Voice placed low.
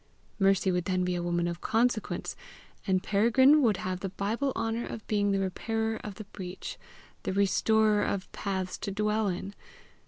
No: high, 200 Hz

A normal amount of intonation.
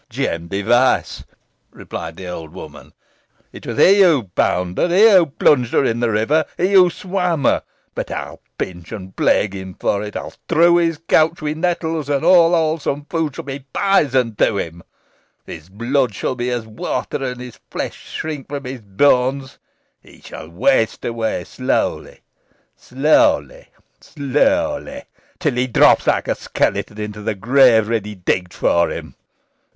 No: wide, 7.3 semitones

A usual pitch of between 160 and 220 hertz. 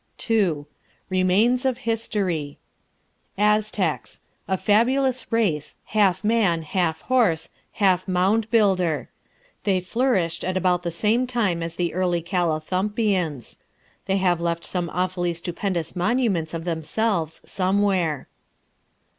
Yes: medium, 185 Hz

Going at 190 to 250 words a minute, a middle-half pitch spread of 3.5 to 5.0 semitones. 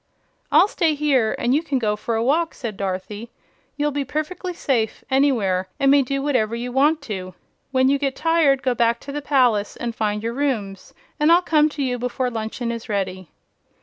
Yes: average, 200 wpm; average, 4.6 semitones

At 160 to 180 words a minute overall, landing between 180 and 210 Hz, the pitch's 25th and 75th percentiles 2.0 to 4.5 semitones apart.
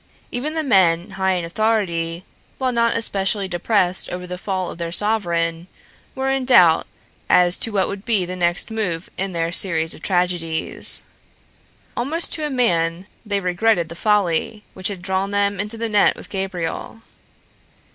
Yes: average, 165 wpm; high, 190 Hz; average, 4.0 semitones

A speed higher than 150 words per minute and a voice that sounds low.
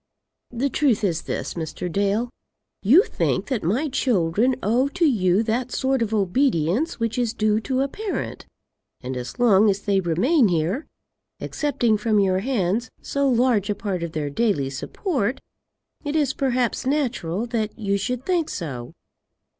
No: average, 160 wpm; high, 225 Hz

